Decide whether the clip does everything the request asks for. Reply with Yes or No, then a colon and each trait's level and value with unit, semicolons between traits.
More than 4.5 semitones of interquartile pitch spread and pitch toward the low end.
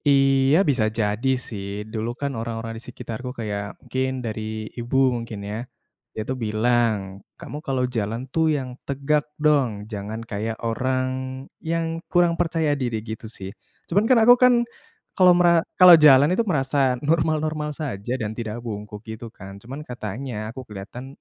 Yes: average, 4.9 semitones; low, 125 Hz